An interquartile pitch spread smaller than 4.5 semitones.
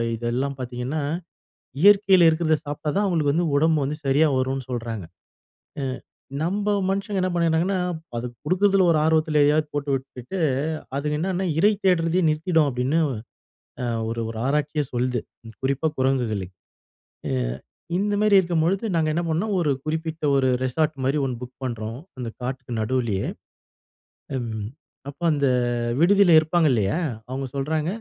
No: average, 4.8 semitones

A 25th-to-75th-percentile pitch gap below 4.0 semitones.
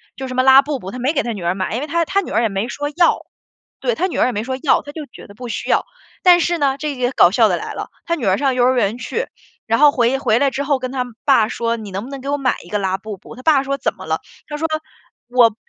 No: average, 4.4 semitones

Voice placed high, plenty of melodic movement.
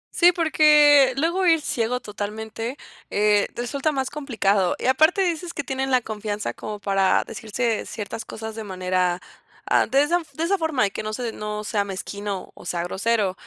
Yes: high, 225 Hz; wide, 6.0 semitones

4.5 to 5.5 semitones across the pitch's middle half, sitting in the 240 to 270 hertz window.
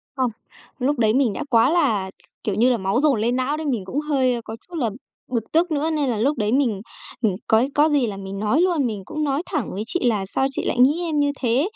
Yes: average, 4.9 semitones; very high, 255 Hz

